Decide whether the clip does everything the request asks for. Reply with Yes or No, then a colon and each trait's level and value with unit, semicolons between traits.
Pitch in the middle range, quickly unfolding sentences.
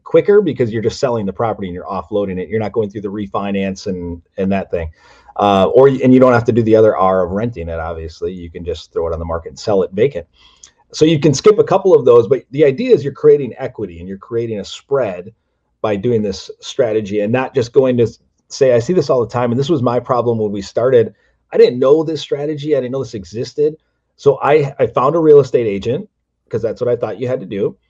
No: low, 120 Hz; fast, 255 wpm